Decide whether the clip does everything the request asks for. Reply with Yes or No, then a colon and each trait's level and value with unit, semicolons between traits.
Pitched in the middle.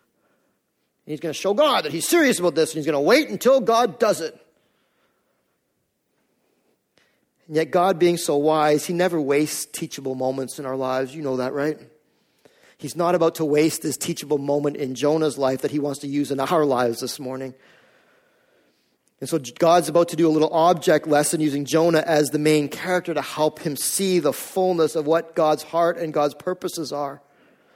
Yes: medium, 155 Hz